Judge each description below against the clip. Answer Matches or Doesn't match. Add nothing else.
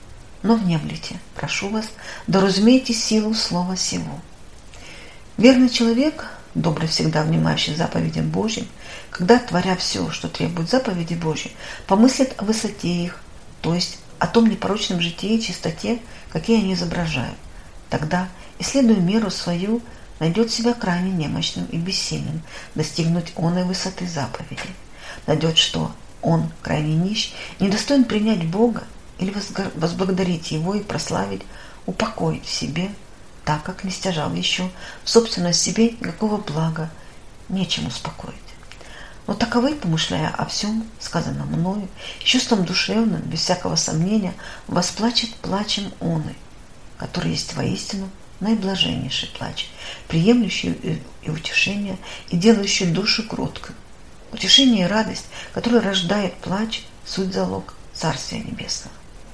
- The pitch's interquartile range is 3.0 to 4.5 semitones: Doesn't match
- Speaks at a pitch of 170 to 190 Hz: Matches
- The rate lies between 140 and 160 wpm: Doesn't match